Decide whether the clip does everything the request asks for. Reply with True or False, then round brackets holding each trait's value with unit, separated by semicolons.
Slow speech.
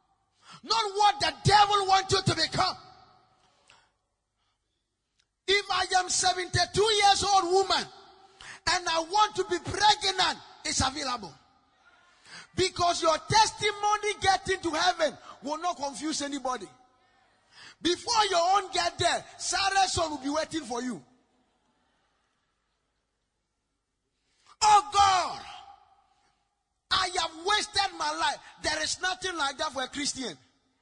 True (115 wpm)